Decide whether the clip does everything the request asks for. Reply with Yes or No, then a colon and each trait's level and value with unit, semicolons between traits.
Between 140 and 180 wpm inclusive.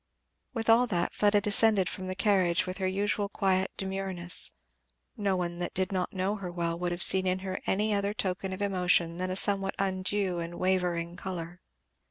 No: average, 190 wpm